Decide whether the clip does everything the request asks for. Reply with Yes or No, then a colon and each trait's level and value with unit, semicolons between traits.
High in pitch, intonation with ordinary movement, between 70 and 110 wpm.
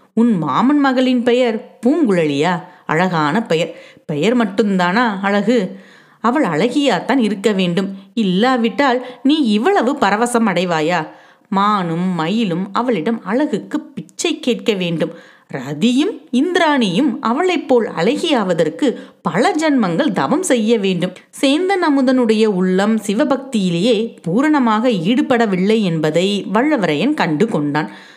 No: high, 230 Hz; wide, 5.7 semitones; average, 100 wpm